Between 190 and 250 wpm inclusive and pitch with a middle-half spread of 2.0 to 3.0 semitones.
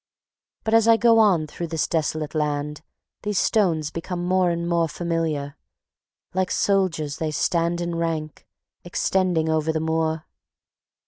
No: average, 140 wpm; narrow, 2.6 semitones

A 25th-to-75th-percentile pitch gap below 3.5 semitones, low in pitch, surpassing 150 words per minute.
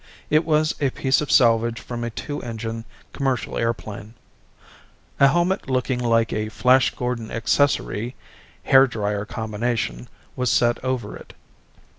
No: average, 2.9 semitones; low, 120 Hz; slow, 135 wpm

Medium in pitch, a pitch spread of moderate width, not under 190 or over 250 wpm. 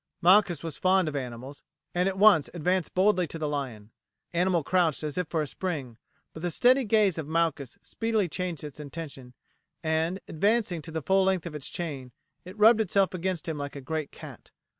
Yes: medium, 165 Hz; average, 4.1 semitones; average, 200 wpm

